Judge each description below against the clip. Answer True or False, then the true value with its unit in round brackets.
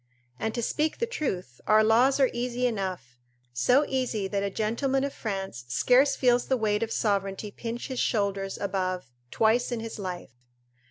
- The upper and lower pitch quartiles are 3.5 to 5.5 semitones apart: True (4.3 semitones)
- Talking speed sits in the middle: True (170 wpm)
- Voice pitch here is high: True (220 Hz)